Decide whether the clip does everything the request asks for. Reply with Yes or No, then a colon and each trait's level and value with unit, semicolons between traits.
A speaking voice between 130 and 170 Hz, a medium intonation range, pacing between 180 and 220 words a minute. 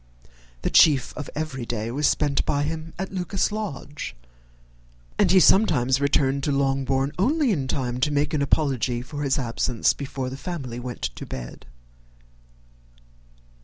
No: medium, 140 Hz; average, 3.2 semitones; average, 150 wpm